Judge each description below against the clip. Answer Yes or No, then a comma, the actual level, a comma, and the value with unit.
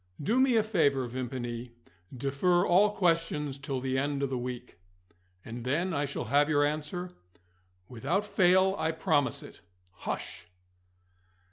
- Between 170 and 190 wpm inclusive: No, average, 140 wpm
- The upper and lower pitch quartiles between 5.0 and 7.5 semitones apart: Yes, average, 5.3 semitones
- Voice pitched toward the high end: No, medium, 145 Hz